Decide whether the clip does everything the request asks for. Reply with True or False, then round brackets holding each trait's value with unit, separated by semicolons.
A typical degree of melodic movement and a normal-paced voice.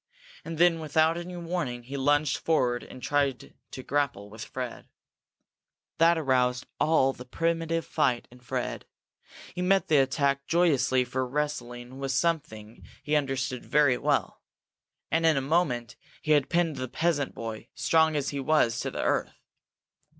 True (4.2 semitones; 155 wpm)